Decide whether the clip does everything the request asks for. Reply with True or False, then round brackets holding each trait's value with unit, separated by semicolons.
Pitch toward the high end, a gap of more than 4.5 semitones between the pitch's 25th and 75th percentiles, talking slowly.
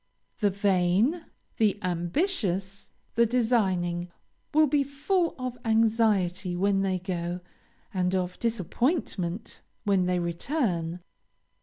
True (195 Hz; 4.9 semitones; 105 wpm)